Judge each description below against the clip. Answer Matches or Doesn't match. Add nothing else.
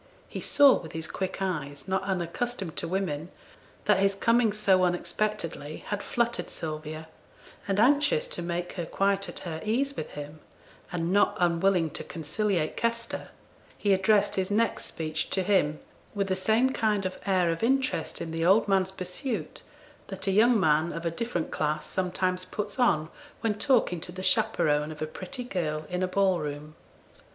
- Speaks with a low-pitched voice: Doesn't match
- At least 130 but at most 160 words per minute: Doesn't match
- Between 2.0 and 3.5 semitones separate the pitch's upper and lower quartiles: Doesn't match